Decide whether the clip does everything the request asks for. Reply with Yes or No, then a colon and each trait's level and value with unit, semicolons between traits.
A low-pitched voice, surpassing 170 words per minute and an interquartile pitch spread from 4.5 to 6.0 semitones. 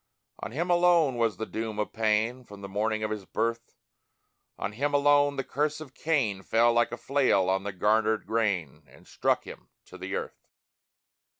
Yes: low, 115 Hz; average, 185 wpm; average, 4.9 semitones